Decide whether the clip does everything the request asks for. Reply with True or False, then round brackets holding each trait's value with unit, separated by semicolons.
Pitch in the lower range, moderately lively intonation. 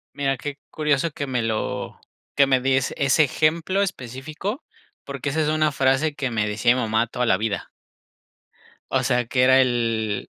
True (130 Hz; 3.7 semitones)